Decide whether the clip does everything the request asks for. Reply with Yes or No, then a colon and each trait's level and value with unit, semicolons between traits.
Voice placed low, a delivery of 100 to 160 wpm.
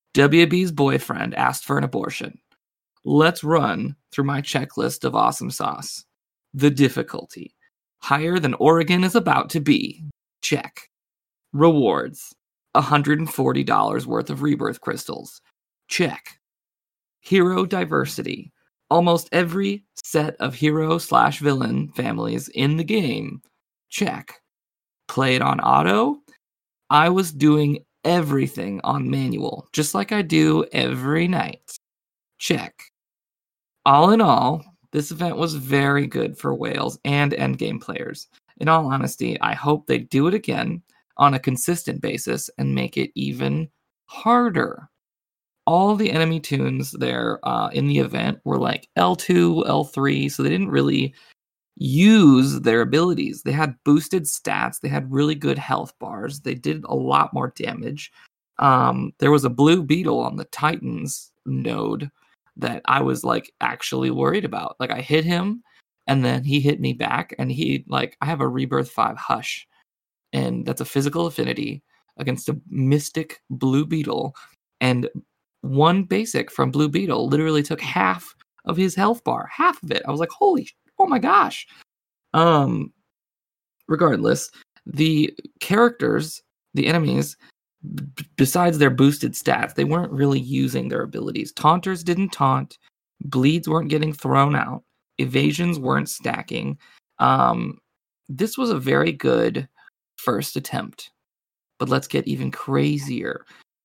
No: medium, 150 Hz; average, 140 wpm